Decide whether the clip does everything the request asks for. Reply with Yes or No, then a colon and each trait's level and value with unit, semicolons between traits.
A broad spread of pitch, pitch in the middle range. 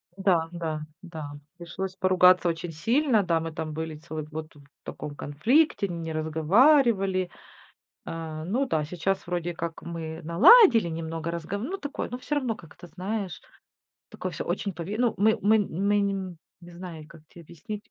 No: average, 4.1 semitones; medium, 175 Hz